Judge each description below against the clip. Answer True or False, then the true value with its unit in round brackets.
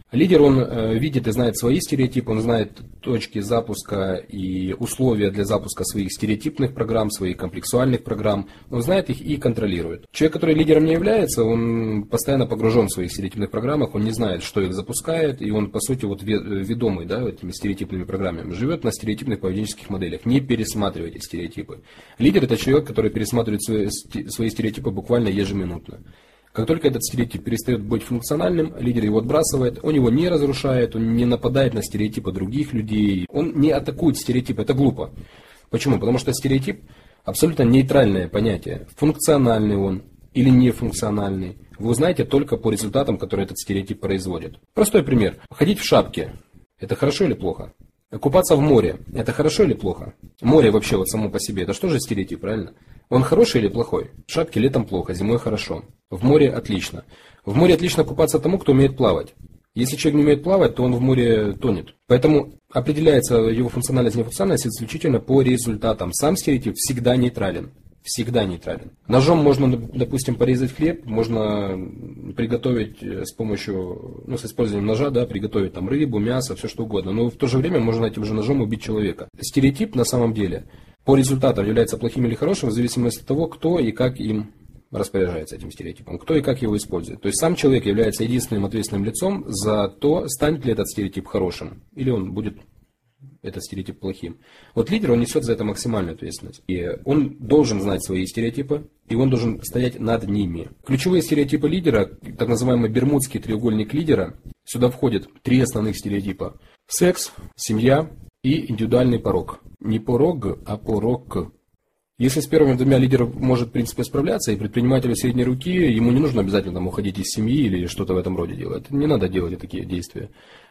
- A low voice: True (115 Hz)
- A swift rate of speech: True (170 wpm)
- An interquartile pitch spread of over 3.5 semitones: True (4.4 semitones)